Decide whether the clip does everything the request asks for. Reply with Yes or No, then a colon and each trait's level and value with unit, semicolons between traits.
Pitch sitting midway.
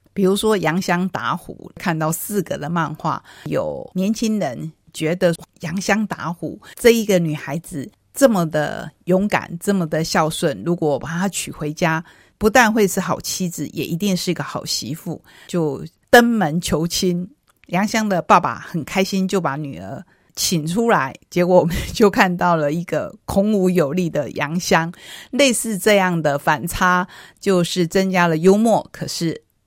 Yes: medium, 175 Hz